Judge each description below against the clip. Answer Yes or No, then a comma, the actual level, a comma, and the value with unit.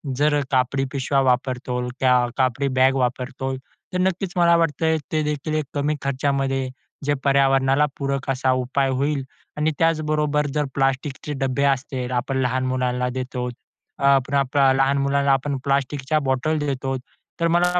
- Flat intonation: Yes, narrow, 2.1 semitones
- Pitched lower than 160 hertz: Yes, low, 135 Hz